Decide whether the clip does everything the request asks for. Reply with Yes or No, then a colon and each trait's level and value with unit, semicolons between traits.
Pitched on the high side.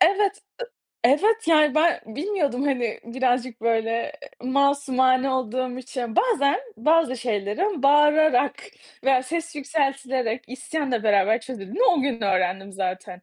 Yes: very high, 260 Hz